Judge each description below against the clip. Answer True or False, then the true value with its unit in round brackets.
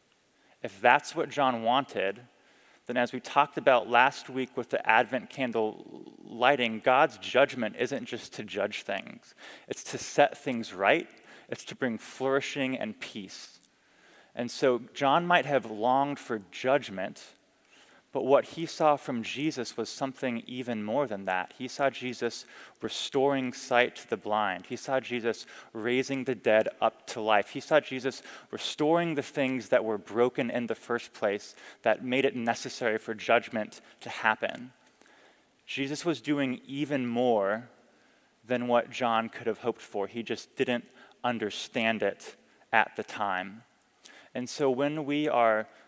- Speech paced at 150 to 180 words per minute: True (155 wpm)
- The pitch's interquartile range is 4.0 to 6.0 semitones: False (2.9 semitones)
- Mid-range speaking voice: False (125 Hz)